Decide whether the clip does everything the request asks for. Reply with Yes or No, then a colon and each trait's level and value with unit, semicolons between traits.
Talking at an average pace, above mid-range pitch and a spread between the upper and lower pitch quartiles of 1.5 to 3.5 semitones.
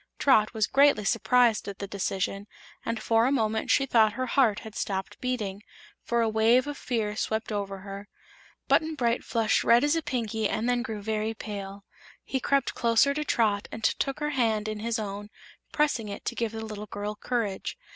Yes: average, 195 wpm; high, 220 Hz; average, 3.0 semitones